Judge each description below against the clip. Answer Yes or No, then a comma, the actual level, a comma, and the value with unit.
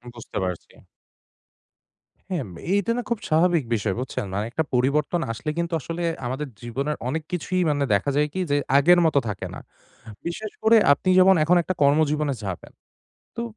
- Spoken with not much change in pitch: No, wide, 5.4 semitones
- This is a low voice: No, medium, 150 Hz